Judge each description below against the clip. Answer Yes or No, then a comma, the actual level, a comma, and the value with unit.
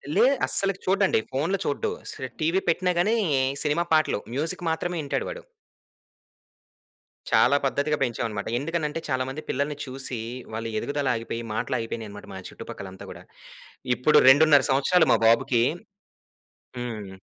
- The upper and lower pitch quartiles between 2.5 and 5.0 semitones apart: No, wide, 5.5 semitones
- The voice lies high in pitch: No, medium, 145 Hz